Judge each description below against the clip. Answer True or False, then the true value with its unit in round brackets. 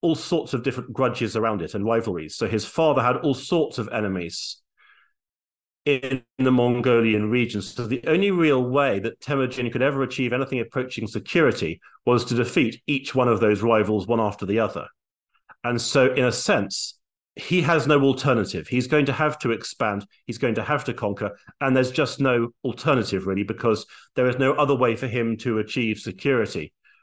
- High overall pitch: False (125 Hz)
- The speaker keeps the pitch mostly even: False (3.2 semitones)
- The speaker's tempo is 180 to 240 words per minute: True (185 wpm)